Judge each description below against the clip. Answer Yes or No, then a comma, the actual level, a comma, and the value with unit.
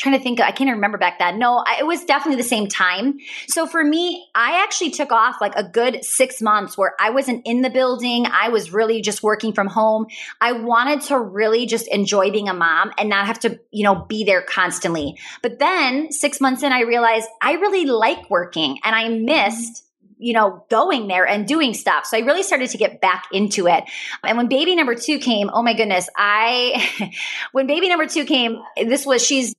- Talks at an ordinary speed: No, fast, 215 wpm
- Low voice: No, high, 235 Hz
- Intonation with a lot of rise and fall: No, average, 4.6 semitones